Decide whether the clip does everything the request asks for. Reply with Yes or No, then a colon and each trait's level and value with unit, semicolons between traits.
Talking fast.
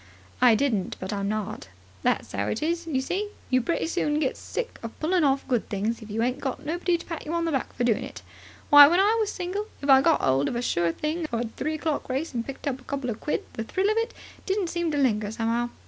Yes: fast, 265 wpm